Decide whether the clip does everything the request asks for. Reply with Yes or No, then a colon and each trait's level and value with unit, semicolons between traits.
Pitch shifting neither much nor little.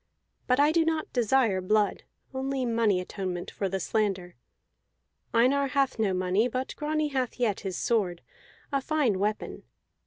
No: wide, 5.7 semitones